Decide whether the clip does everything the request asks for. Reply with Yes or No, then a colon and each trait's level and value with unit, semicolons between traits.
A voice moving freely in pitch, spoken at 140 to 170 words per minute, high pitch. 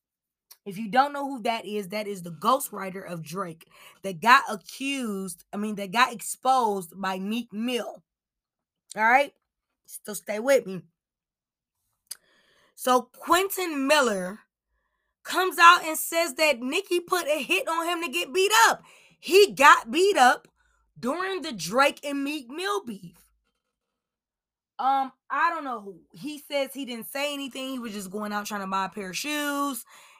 Yes: wide, 7.1 semitones; average, 165 wpm; very high, 265 Hz